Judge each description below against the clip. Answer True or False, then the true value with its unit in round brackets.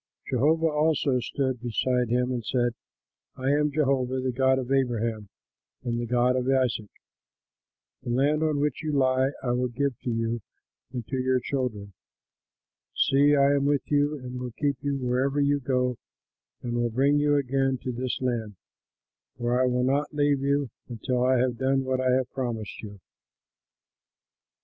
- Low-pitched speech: True (130 Hz)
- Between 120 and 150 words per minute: False (170 wpm)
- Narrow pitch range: True (2.3 semitones)